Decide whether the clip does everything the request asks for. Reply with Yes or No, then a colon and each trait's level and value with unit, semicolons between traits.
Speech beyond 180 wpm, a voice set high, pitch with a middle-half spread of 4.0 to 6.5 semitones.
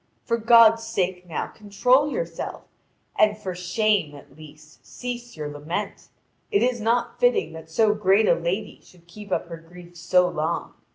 No: average, 165 wpm; high, 195 Hz; average, 5.0 semitones